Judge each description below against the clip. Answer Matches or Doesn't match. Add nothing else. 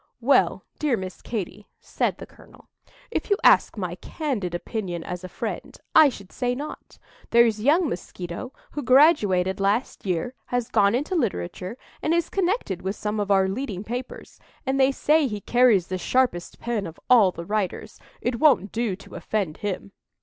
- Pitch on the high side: Matches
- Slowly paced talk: Doesn't match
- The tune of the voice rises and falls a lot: Matches